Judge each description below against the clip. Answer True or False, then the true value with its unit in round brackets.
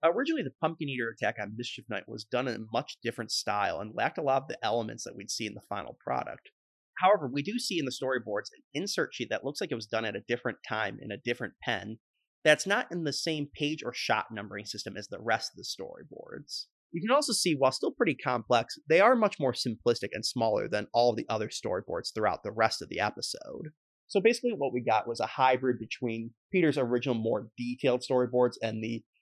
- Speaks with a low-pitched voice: True (125 Hz)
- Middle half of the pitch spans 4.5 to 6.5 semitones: True (4.8 semitones)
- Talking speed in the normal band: False (230 wpm)